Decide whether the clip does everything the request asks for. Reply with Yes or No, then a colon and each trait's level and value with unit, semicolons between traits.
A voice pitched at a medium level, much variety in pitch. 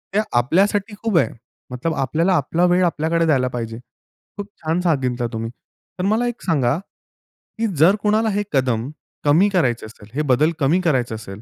Yes: medium, 155 Hz; wide, 6.9 semitones